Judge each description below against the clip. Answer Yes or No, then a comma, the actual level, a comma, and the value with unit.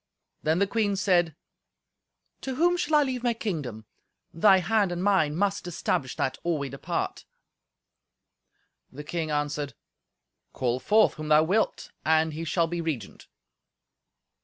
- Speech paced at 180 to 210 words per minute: No, average, 140 wpm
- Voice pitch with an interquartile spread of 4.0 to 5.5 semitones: Yes, average, 5.2 semitones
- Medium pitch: Yes, medium, 170 Hz